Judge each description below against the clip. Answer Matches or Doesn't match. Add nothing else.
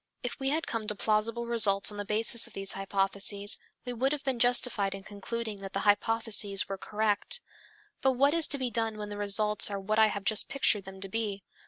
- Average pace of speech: Doesn't match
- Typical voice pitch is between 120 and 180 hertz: Doesn't match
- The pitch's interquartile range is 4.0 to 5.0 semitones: Doesn't match